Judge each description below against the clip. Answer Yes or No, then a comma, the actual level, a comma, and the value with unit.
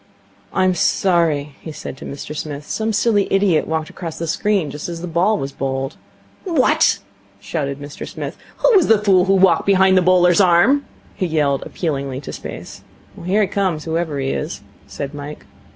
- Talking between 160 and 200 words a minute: Yes, average, 180 wpm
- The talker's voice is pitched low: No, medium, 170 Hz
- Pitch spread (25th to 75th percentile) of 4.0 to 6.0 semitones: Yes, average, 4.8 semitones